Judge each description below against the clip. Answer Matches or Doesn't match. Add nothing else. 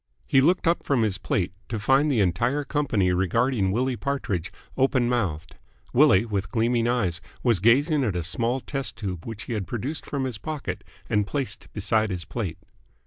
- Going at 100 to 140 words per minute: Doesn't match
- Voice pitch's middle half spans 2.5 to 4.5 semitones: Doesn't match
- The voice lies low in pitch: Matches